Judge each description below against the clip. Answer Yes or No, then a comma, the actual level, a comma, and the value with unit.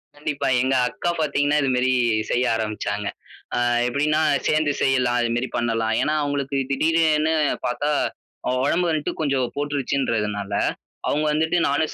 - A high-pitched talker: No, medium, 140 Hz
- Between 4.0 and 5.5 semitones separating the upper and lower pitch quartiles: No, average, 3.6 semitones